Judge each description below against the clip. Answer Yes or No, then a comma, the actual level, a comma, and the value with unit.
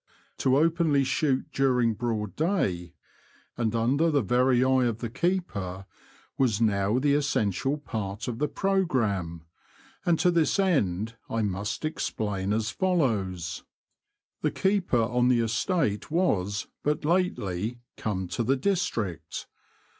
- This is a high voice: No, low, 120 Hz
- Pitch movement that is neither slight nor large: No, wide, 6.5 semitones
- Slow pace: Yes, slow, 130 wpm